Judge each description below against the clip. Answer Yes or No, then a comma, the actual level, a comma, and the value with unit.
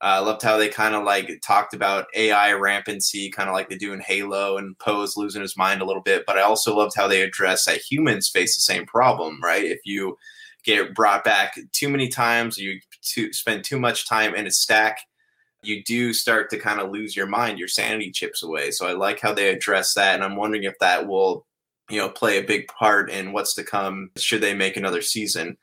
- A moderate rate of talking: No, fast, 230 wpm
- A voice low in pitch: Yes, low, 105 Hz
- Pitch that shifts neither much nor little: No, narrow, 2.0 semitones